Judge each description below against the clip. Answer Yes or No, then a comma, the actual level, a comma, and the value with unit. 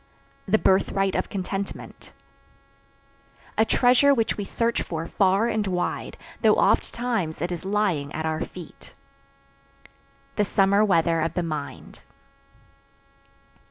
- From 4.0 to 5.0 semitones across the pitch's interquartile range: Yes, average, 4.4 semitones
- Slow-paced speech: Yes, slow, 125 wpm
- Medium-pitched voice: No, high, 195 Hz